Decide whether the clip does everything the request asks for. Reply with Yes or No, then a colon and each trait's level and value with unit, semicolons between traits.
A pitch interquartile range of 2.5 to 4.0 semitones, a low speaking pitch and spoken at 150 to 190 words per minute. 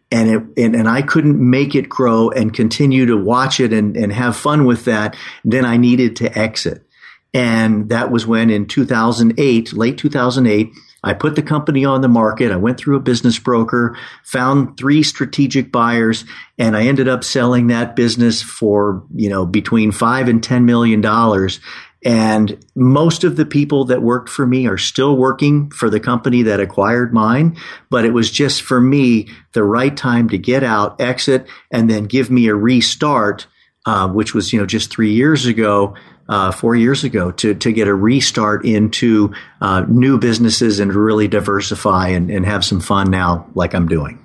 Yes: average, 3.1 semitones; low, 115 Hz; average, 185 wpm